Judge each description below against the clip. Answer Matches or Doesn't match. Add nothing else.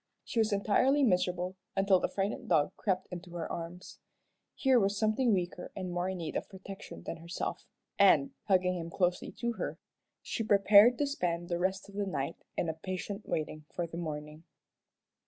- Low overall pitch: Doesn't match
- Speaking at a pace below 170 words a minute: Doesn't match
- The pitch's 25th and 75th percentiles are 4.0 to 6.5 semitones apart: Doesn't match